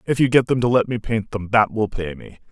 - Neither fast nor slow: No, fast, 310 wpm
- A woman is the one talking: No, male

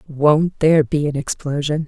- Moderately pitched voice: Yes, medium, 150 Hz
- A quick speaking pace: No, average, 160 wpm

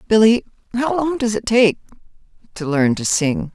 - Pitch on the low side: No, high, 215 Hz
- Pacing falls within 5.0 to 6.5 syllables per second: No, 4.7 syllables/s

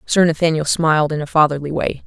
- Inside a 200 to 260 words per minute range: Yes, fast, 205 wpm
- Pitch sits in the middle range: Yes, medium, 155 Hz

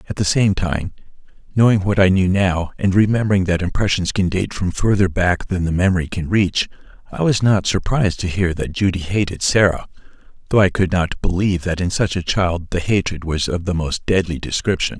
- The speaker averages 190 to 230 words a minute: Yes, fast, 205 wpm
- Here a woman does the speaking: No, male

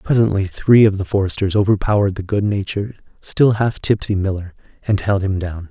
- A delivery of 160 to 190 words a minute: Yes, average, 170 wpm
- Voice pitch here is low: Yes, low, 100 Hz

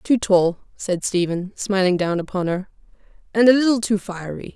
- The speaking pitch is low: No, high, 195 Hz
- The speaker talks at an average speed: Yes, average, 170 wpm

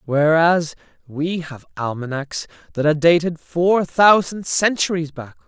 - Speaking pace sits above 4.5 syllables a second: No, 4.4 syllables/s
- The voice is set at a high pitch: No, medium, 160 Hz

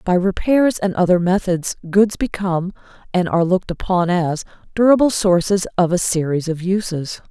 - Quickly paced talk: No, average, 155 wpm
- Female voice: Yes, female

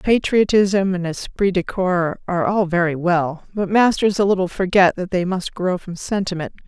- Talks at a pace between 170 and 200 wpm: Yes, average, 180 wpm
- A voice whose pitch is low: No, medium, 185 Hz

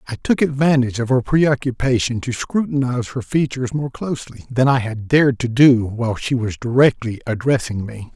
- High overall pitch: No, low, 125 Hz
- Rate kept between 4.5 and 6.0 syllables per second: Yes, 5.4 syllables/s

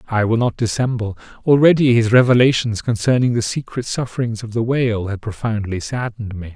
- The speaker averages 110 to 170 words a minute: Yes, average, 165 wpm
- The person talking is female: No, male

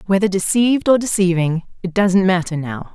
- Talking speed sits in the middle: Yes, average, 165 wpm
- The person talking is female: Yes, female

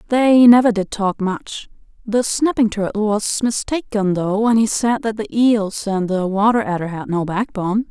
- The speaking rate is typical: Yes, average, 180 wpm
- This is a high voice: Yes, high, 210 Hz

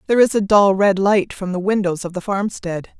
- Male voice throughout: No, female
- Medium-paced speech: No, fast, 240 wpm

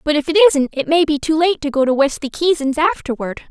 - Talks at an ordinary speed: No, fast, 255 wpm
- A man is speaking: No, female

